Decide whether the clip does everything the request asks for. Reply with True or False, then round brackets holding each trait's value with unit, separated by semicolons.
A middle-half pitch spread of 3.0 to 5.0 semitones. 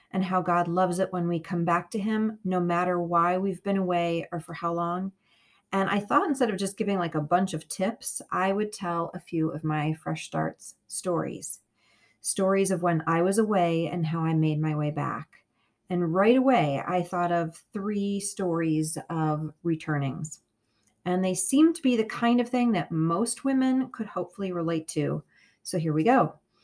True (3.4 semitones)